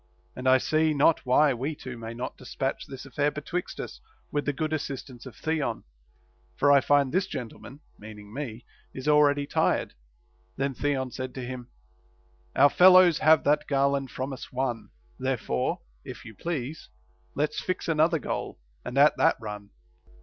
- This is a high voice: No, medium, 140 Hz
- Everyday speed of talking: Yes, average, 165 wpm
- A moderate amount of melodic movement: Yes, average, 3.0 semitones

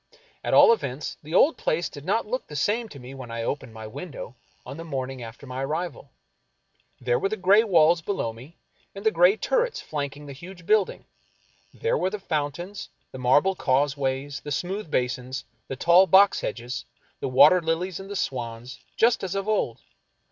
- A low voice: No, medium, 155 Hz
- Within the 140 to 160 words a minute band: No, average, 190 wpm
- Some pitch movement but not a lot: No, wide, 6.6 semitones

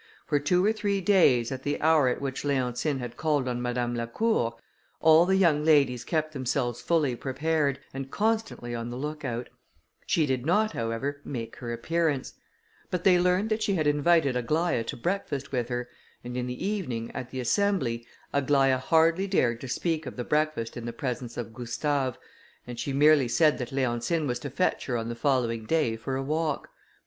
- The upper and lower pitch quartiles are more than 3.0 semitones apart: Yes, average, 4.8 semitones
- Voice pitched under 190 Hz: Yes, medium, 140 Hz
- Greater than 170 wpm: Yes, average, 190 wpm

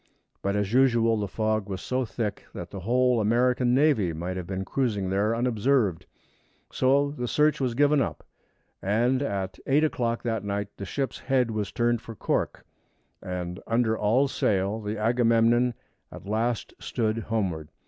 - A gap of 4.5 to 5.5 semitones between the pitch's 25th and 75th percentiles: No, average, 3.8 semitones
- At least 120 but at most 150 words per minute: No, average, 160 wpm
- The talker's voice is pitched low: Yes, low, 115 Hz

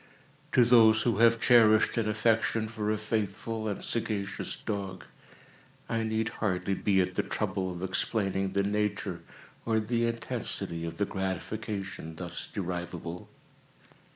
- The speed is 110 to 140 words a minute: Yes, slow, 135 wpm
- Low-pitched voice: Yes, low, 105 Hz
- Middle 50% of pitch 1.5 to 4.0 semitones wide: Yes, average, 2.8 semitones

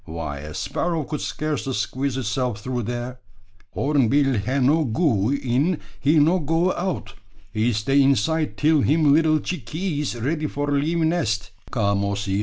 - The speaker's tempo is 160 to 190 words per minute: No, average, 150 wpm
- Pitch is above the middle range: No, medium, 140 Hz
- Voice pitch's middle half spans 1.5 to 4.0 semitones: No, average, 5.3 semitones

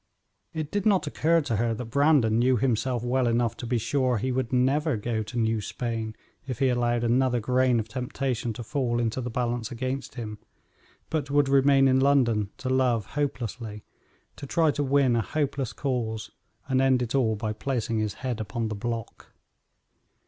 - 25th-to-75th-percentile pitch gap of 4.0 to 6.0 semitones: No, average, 2.9 semitones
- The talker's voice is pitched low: Yes, low, 125 Hz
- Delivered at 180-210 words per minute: Yes, average, 185 wpm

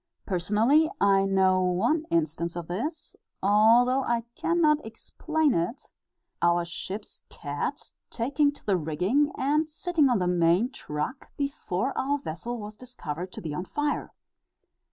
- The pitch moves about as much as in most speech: No, wide, 8.0 semitones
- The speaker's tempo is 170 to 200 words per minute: No, average, 140 wpm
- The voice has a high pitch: Yes, high, 220 Hz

